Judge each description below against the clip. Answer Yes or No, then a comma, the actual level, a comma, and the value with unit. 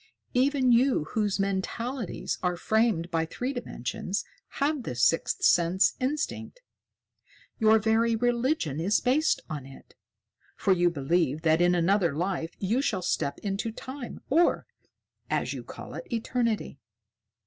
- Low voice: No, high, 210 Hz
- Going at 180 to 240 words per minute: No, slow, 135 wpm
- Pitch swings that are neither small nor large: No, wide, 6.3 semitones